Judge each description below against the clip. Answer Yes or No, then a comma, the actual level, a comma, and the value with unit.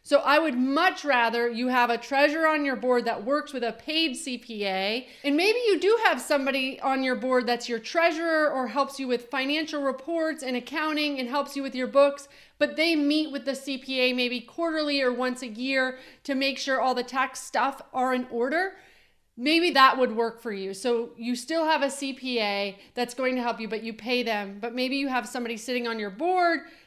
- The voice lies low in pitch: No, very high, 265 Hz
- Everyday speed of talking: No, fast, 215 wpm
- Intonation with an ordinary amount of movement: Yes, average, 3.3 semitones